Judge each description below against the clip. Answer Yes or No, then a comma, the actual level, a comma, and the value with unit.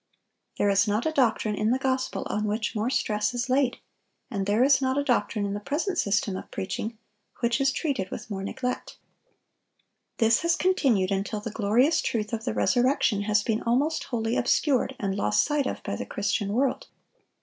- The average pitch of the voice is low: No, high, 230 Hz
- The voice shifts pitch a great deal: No, average, 4.3 semitones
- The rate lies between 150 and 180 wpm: No, average, 190 wpm